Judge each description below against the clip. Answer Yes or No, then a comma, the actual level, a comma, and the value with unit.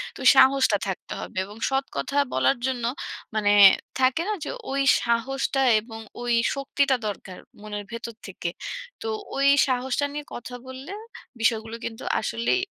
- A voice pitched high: Yes, high, 245 Hz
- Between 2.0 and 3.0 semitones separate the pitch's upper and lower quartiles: No, average, 3.5 semitones